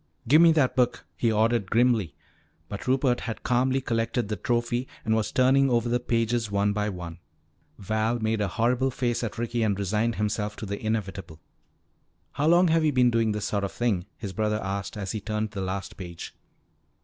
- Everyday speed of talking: Yes, average, 195 wpm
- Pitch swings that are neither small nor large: Yes, average, 3.1 semitones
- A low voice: Yes, low, 110 Hz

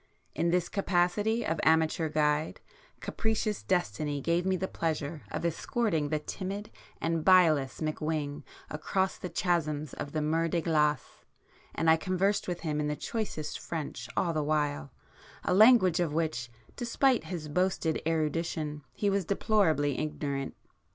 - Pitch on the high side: No, medium, 160 Hz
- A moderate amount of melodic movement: Yes, average, 3.5 semitones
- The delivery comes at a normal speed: Yes, average, 145 wpm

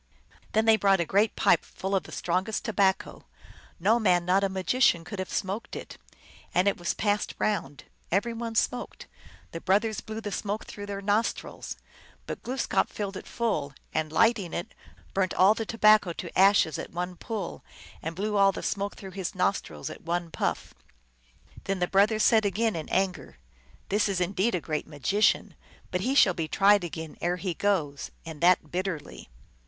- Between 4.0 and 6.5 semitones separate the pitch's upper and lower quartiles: No, average, 3.2 semitones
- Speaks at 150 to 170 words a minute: No, average, 185 wpm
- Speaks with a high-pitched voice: Yes, high, 195 Hz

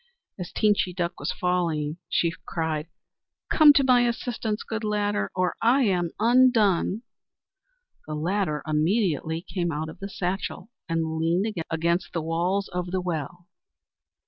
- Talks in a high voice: No, medium, 180 Hz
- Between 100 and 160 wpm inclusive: Yes, average, 140 wpm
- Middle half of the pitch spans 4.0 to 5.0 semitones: Yes, average, 4.3 semitones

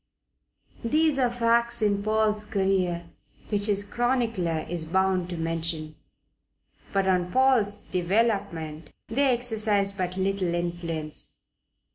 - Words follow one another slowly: Yes, slow, 110 wpm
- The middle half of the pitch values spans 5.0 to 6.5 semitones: No, average, 4.6 semitones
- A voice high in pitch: Yes, high, 195 Hz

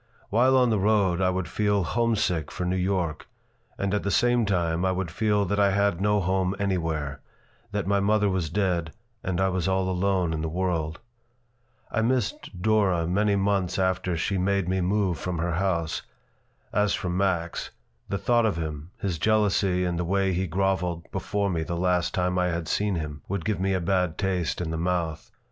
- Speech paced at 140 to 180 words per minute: No, average, 195 wpm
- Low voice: Yes, very low, 95 Hz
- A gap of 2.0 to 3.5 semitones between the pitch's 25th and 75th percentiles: Yes, narrow, 2.5 semitones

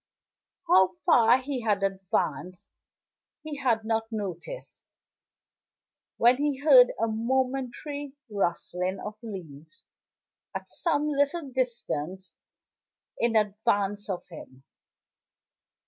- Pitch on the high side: Yes, high, 225 Hz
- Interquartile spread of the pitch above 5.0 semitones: Yes, wide, 5.5 semitones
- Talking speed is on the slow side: Yes, slow, 95 wpm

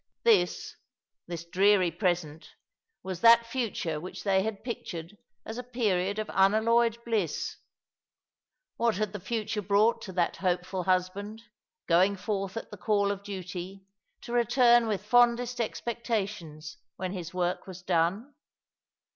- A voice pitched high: Yes, high, 200 Hz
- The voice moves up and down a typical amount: Yes, average, 4.0 semitones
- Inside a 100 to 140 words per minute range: Yes, slow, 135 wpm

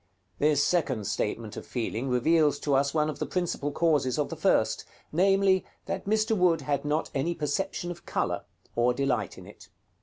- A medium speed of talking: Yes, average, 180 wpm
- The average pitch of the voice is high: No, medium, 150 Hz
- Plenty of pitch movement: No, average, 4.7 semitones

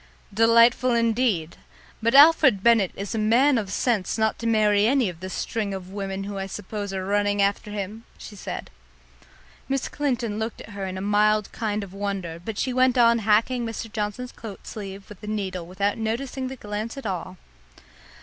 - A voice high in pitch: Yes, high, 210 Hz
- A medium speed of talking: Yes, average, 190 wpm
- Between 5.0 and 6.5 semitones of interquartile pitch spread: No, average, 2.8 semitones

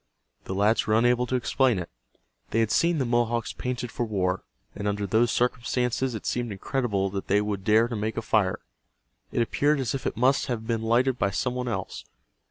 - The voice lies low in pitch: Yes, low, 115 Hz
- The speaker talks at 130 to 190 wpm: No, fast, 205 wpm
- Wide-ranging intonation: No, average, 3.1 semitones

